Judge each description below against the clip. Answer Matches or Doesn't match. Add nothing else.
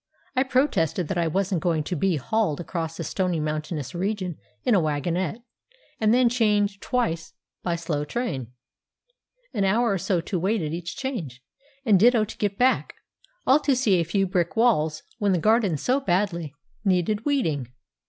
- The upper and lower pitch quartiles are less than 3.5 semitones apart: Doesn't match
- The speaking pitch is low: Doesn't match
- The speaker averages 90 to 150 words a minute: Doesn't match